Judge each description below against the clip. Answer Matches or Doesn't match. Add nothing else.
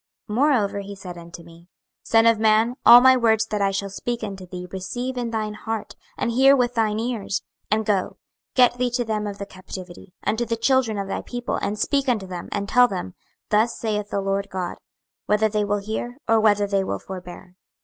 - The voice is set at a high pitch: Matches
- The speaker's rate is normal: Doesn't match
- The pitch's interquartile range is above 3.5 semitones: Doesn't match